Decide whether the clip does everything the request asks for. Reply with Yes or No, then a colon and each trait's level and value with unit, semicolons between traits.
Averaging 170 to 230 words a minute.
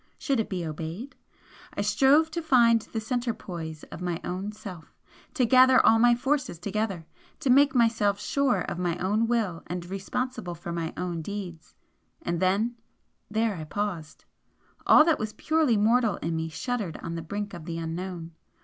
Yes: average, 175 wpm